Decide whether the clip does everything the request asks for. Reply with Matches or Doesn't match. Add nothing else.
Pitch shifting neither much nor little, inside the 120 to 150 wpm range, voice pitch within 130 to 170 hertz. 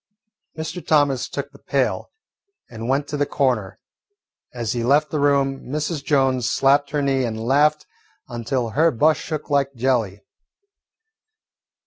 Matches